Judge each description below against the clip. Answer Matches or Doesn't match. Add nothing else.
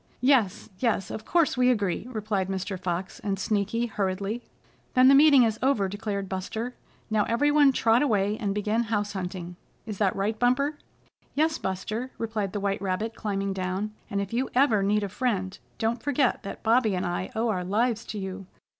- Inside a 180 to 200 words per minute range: Matches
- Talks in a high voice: Matches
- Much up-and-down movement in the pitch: Doesn't match